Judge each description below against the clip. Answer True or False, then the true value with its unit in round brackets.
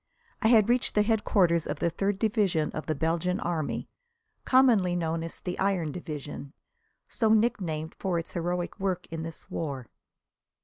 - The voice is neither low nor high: True (175 Hz)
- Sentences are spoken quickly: False (160 wpm)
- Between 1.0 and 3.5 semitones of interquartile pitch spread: False (4.1 semitones)